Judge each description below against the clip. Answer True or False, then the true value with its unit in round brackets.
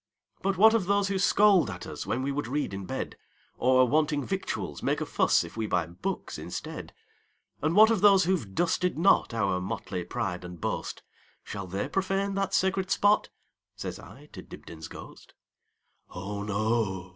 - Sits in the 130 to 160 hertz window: True (140 Hz)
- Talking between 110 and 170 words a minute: True (150 wpm)